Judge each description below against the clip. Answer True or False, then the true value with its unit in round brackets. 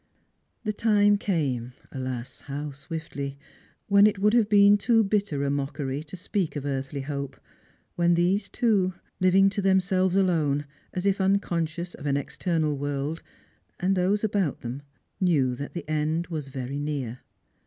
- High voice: False (165 Hz)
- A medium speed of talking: True (165 wpm)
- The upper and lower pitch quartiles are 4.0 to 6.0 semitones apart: True (5.6 semitones)